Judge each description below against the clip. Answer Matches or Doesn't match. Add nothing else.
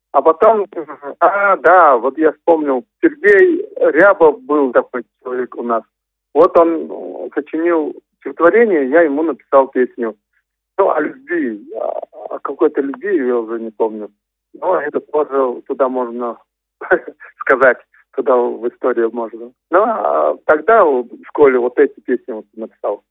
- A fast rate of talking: Doesn't match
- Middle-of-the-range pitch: Matches